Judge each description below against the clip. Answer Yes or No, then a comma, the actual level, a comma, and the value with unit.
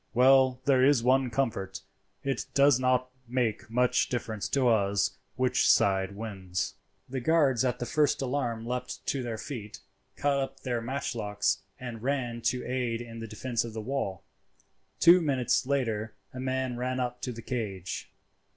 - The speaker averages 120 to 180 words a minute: Yes, average, 160 wpm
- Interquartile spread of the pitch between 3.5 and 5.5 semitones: No, average, 2.8 semitones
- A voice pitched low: Yes, low, 125 Hz